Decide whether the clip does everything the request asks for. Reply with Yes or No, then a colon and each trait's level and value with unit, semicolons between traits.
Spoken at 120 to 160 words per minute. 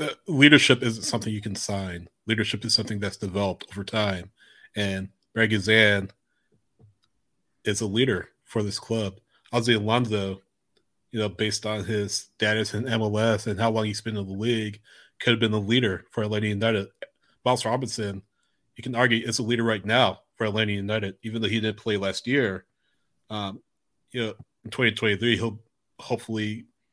No: average, 175 wpm